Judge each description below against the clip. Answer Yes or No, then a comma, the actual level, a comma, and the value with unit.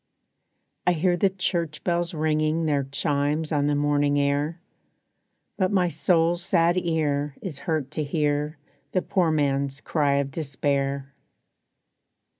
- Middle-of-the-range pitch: Yes, medium, 150 Hz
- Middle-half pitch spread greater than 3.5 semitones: No, average, 2.9 semitones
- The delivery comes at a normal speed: No, slow, 130 wpm